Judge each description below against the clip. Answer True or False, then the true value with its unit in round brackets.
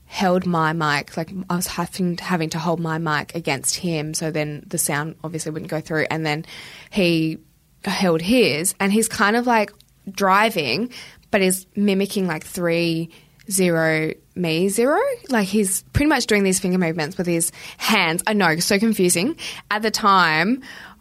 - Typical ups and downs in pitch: True (4.2 semitones)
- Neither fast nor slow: True (175 wpm)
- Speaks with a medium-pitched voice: True (180 Hz)